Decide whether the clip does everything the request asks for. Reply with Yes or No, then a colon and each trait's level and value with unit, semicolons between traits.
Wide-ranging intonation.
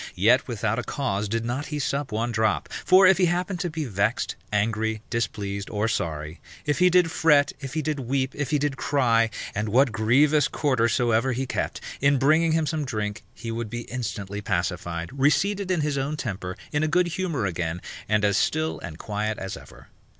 Yes: wide, 5.9 semitones